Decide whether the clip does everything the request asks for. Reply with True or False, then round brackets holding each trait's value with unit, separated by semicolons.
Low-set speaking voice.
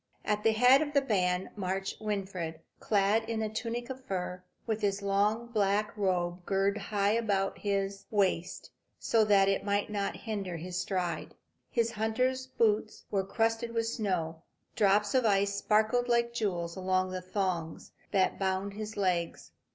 False (200 Hz)